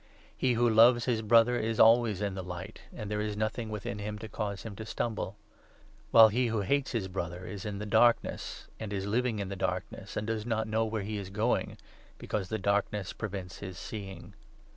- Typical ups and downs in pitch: No, narrow, 2.2 semitones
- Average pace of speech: No, fast, 220 wpm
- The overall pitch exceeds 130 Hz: No, low, 105 Hz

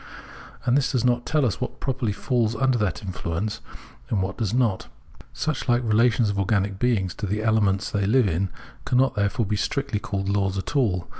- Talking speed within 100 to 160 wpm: No, average, 200 wpm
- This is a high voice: No, low, 110 Hz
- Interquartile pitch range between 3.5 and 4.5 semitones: Yes, average, 4.0 semitones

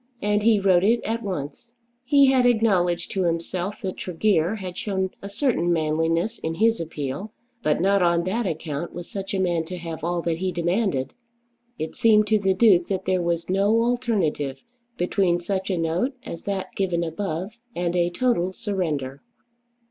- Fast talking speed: No, average, 175 wpm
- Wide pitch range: No, average, 3.6 semitones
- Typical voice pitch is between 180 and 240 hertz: Yes, medium, 185 Hz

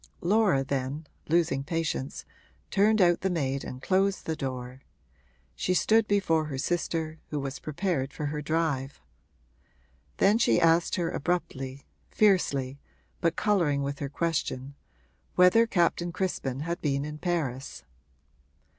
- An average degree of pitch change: Yes, average, 4.4 semitones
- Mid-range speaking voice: Yes, medium, 160 Hz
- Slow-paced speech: Yes, slow, 130 wpm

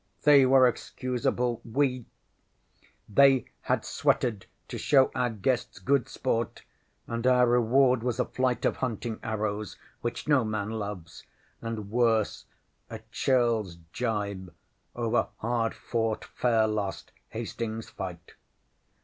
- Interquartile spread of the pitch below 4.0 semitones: Yes, average, 2.7 semitones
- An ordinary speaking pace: No, slow, 120 wpm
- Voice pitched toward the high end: No, low, 115 Hz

